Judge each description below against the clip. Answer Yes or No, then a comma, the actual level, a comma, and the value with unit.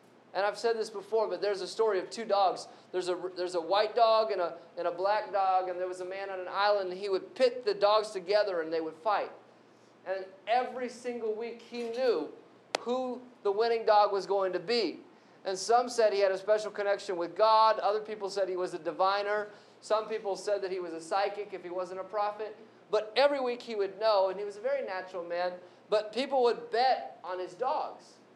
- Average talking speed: No, fast, 225 wpm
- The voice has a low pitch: No, high, 205 Hz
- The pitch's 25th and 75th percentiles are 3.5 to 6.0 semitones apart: No, average, 2.9 semitones